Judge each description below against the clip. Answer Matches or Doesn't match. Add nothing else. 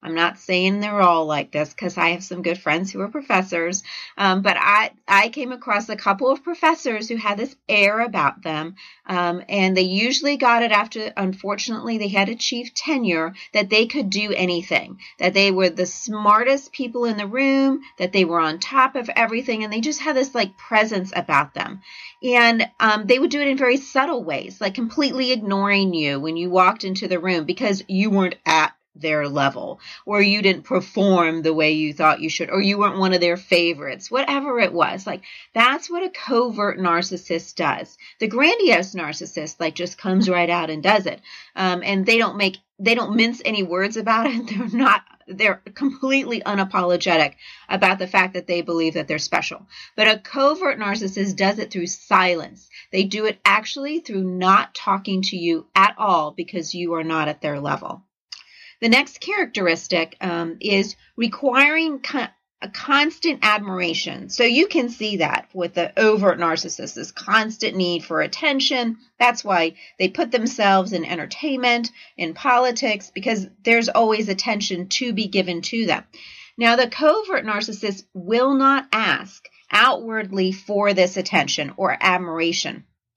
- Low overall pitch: Doesn't match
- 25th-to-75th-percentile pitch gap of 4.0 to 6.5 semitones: Matches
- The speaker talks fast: Doesn't match